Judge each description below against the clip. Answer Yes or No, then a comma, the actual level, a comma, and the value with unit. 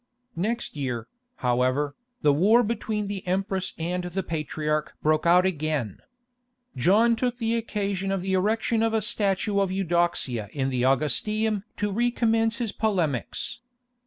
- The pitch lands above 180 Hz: Yes, high, 190 Hz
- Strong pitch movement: Yes, wide, 6.2 semitones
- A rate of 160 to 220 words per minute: No, average, 140 wpm